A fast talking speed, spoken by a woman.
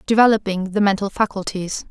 No: slow, 125 wpm; female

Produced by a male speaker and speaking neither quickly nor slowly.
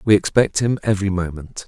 Yes: male; average, 180 wpm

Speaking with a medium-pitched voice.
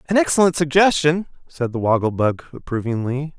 Yes: medium, 145 Hz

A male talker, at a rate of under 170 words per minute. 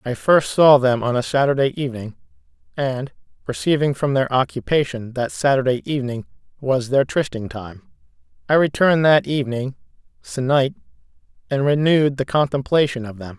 Yes: male; average, 140 wpm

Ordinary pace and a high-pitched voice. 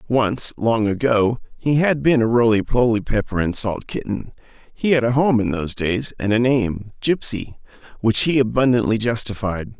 No: average, 170 wpm; low, 115 Hz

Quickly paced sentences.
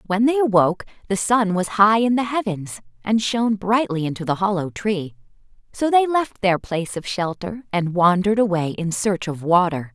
No: average, 185 wpm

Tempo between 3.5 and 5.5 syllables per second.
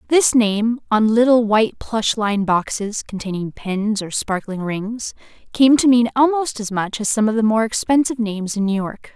Yes: 4.9 syllables/s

